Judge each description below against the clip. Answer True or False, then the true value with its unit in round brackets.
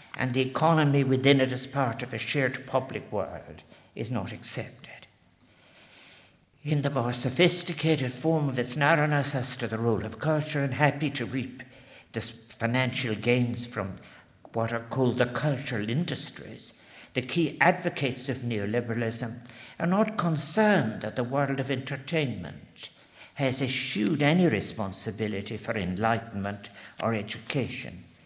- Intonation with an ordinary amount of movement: True (4.0 semitones)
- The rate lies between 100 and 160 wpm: True (135 wpm)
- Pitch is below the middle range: True (130 Hz)